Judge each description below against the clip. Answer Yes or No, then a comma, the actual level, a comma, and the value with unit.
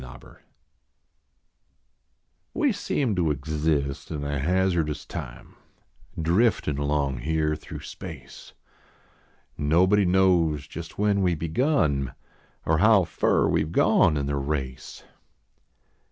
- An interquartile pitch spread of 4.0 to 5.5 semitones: Yes, average, 4.4 semitones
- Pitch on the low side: Yes, very low, 80 Hz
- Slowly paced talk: Yes, slow, 110 wpm